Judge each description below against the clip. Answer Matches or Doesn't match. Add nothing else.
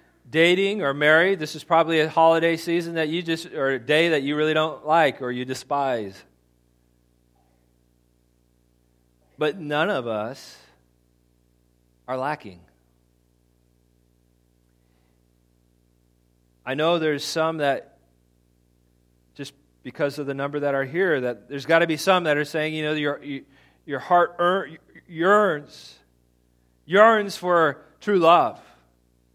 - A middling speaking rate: Doesn't match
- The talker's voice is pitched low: Matches